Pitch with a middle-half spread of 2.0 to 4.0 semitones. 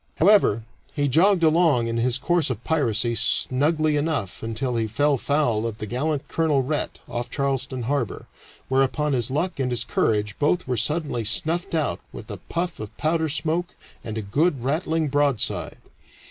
No: average, 5.0 semitones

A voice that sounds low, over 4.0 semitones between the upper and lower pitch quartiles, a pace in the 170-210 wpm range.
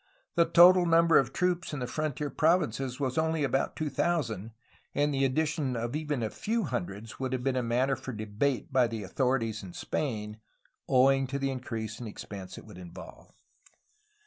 Yes: low, 130 Hz; average, 4.8 semitones; average, 180 wpm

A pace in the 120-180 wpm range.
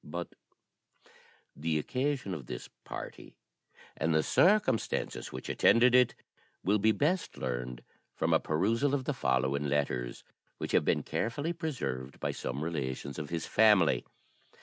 Yes: average, 140 wpm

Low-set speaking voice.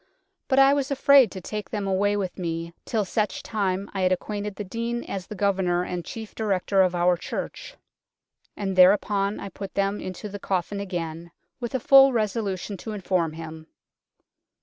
No: high, 195 Hz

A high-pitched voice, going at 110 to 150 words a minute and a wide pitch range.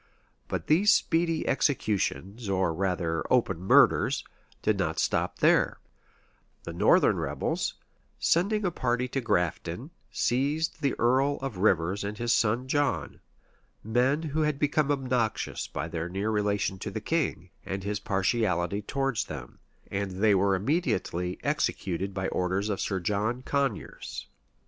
No: low, 105 Hz; average, 140 wpm; wide, 6.3 semitones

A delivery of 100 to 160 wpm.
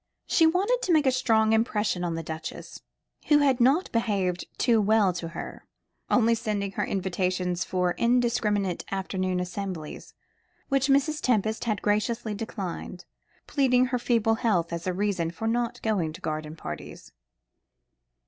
Yes: average, 150 wpm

